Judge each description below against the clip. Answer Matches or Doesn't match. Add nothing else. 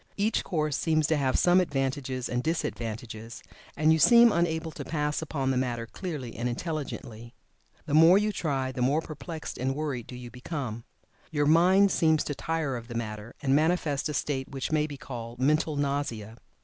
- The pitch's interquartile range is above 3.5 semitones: Matches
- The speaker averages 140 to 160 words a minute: Doesn't match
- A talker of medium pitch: Matches